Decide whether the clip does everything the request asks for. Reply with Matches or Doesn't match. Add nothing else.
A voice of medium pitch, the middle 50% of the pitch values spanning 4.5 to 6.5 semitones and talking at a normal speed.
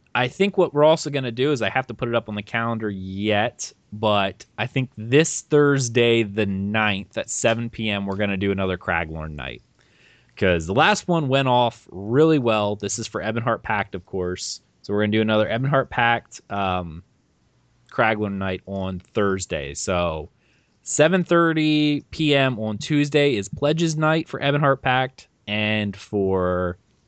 Doesn't match